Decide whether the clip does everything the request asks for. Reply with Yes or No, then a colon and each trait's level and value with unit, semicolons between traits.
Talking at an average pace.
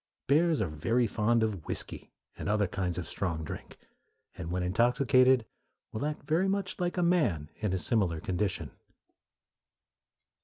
Yes: average, 150 wpm